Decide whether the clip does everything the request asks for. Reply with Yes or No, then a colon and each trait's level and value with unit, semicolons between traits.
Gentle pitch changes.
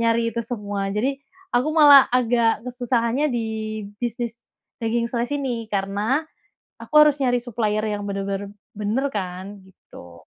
No: average, 3.3 semitones